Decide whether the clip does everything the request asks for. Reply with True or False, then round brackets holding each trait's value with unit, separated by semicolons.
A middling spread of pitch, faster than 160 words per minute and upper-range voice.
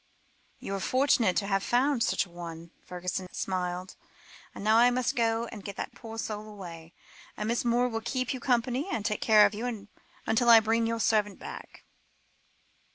True (3.4 semitones; 185 wpm; 220 Hz)